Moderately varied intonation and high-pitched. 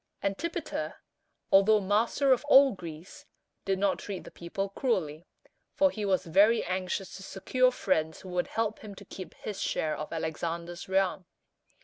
Yes: average, 3.6 semitones; high, 195 Hz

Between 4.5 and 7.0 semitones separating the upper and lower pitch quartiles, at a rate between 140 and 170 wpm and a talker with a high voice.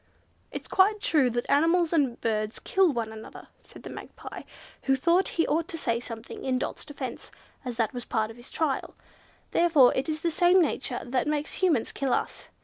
No: wide, 5.6 semitones; average, 200 wpm; very high, 275 Hz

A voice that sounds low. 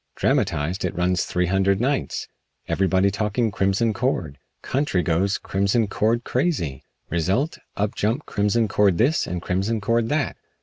Yes: low, 100 Hz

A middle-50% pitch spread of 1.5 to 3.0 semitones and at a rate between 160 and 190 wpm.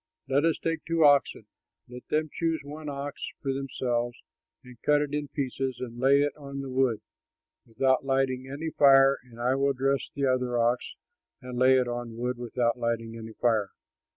Yes: narrow, 2.5 semitones; average, 180 wpm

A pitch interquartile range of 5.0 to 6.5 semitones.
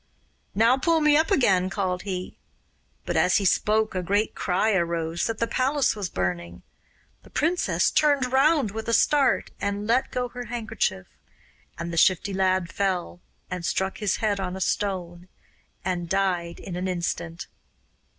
No: average, 4.6 semitones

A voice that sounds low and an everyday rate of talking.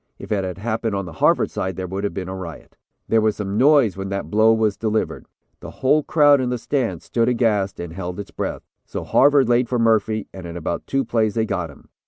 No: low, 110 Hz; fast, 240 wpm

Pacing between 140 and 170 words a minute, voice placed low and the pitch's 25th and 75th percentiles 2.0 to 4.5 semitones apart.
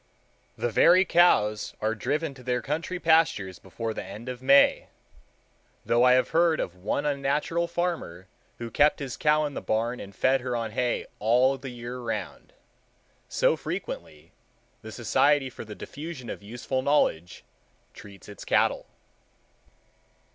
No: average, 150 wpm; low, 130 Hz; average, 5.0 semitones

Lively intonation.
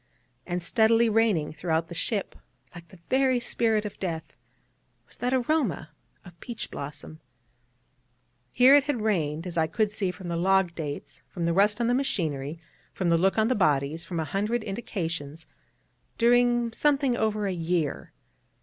Yes: wide, 5.8 semitones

